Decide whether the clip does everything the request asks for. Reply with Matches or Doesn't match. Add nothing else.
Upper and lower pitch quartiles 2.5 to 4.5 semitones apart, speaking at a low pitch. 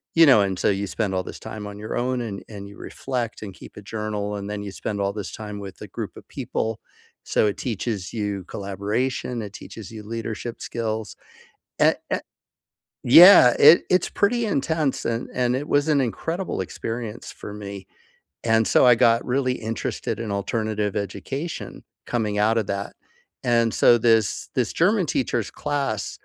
Matches